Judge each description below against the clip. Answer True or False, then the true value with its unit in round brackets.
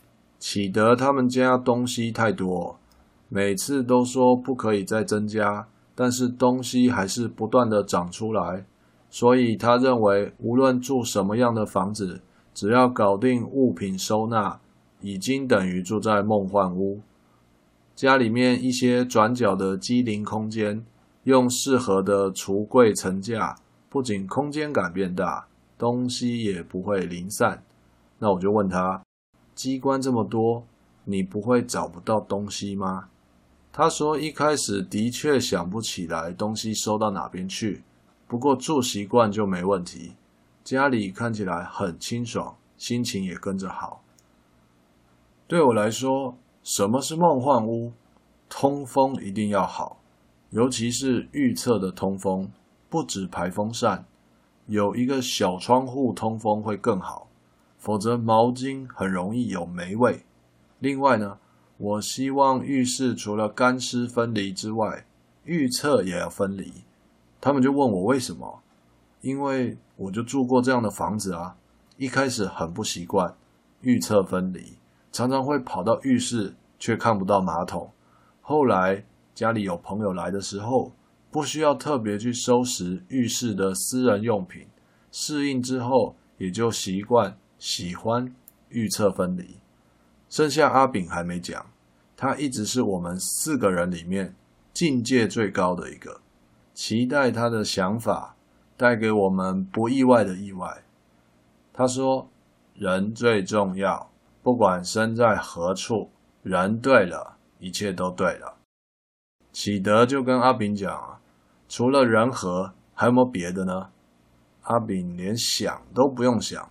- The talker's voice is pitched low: True (105 Hz)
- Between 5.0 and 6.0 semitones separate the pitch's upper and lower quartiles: True (5.6 semitones)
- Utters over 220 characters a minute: False (205 characters per minute)